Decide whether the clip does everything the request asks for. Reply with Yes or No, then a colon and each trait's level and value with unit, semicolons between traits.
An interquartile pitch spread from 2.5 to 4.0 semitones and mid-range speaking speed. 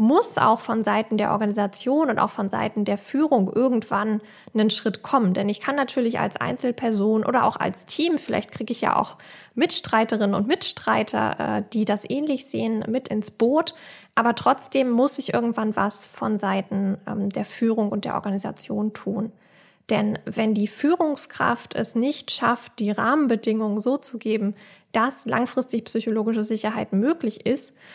Yes: average, 3.5 semitones; average, 155 wpm